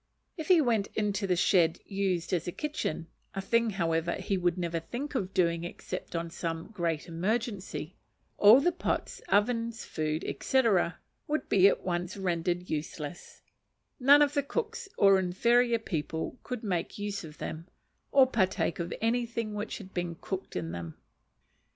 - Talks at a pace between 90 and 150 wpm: No, average, 160 wpm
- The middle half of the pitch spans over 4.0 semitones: Yes, wide, 5.5 semitones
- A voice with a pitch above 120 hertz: Yes, high, 190 Hz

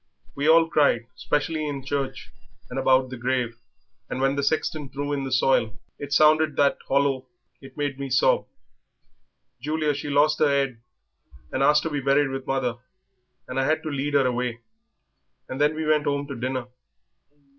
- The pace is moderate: Yes, average, 175 wpm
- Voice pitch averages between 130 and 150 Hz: Yes, medium, 140 Hz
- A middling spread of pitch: No, narrow, 2.0 semitones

